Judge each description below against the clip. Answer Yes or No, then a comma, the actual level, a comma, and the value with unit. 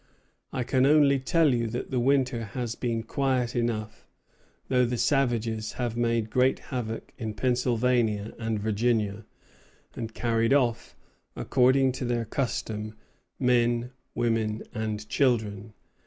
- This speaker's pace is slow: Yes, slow, 125 wpm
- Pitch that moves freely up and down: No, narrow, 2.4 semitones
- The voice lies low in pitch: Yes, low, 120 Hz